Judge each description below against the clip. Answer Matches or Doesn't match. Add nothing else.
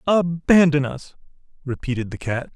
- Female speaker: Doesn't match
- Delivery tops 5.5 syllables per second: Doesn't match